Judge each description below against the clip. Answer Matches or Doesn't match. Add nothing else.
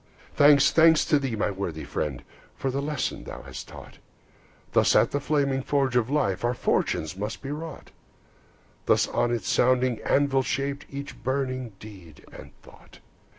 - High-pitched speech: Doesn't match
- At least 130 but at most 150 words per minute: Doesn't match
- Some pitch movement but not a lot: Matches